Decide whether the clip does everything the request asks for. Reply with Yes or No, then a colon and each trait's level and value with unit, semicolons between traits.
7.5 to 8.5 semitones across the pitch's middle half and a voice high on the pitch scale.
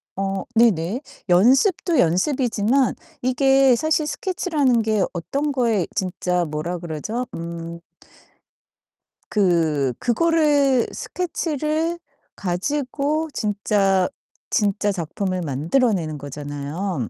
Yes: wide, 8.0 semitones; high, 210 Hz